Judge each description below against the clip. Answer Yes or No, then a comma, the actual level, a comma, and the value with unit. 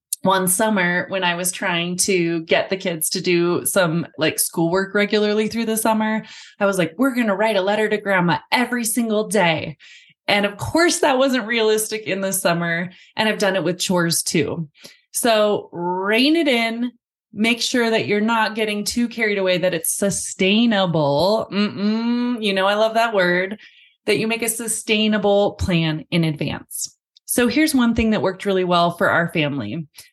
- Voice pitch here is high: Yes, high, 205 Hz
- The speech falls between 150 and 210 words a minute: Yes, average, 180 wpm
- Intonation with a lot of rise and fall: No, average, 3.7 semitones